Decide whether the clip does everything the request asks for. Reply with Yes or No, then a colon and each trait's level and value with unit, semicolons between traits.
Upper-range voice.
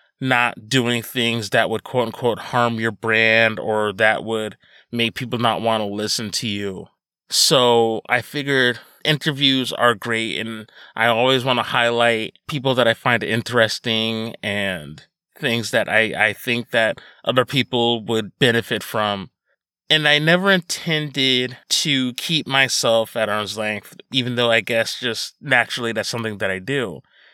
No: low, 115 Hz